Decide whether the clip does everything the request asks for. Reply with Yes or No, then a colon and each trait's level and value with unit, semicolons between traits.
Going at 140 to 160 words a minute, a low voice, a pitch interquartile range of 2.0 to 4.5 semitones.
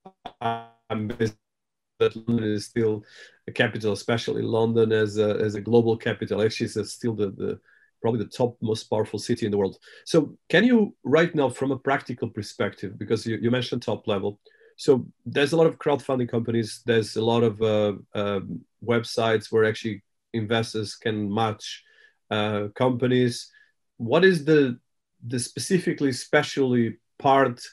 Yes: average, 155 wpm; low, 115 Hz; average, 3.8 semitones